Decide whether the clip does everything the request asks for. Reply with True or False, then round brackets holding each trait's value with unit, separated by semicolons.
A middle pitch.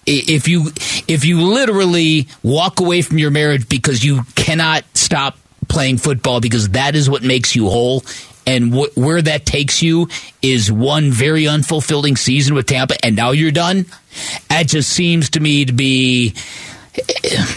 True (145 Hz)